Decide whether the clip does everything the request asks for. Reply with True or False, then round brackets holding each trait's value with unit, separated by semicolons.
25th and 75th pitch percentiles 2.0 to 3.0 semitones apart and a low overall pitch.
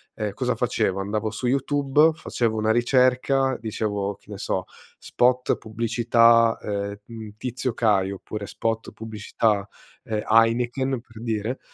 True (2.7 semitones; 115 Hz)